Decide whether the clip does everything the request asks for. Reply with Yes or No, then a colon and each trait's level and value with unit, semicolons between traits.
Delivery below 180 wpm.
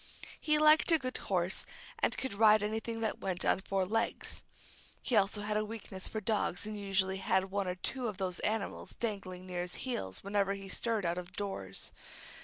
No: average, 195 wpm